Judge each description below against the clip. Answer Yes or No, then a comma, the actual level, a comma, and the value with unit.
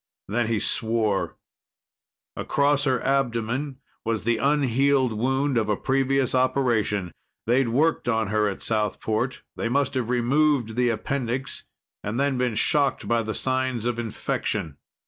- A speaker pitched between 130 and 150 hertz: No, low, 120 Hz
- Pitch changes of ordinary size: Yes, average, 3.4 semitones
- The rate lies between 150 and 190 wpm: No, average, 140 wpm